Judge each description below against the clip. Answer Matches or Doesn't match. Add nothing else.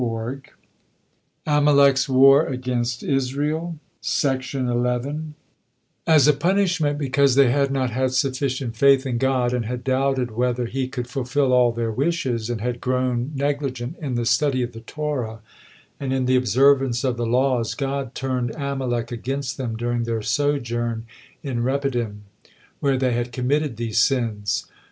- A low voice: Matches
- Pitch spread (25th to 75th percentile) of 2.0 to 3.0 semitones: Matches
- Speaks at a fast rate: Doesn't match